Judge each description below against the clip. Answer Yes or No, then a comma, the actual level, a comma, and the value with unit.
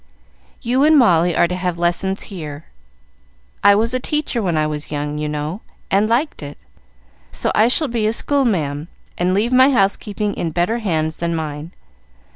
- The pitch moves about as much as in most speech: No, wide, 6.6 semitones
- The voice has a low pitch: No, medium, 185 Hz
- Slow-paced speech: No, average, 180 wpm